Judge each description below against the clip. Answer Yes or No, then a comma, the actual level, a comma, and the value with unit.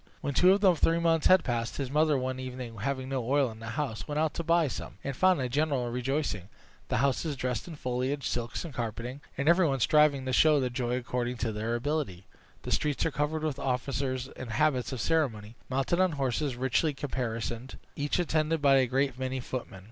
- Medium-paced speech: No, fast, 210 wpm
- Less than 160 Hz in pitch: Yes, low, 135 Hz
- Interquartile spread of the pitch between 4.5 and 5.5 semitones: No, average, 3.5 semitones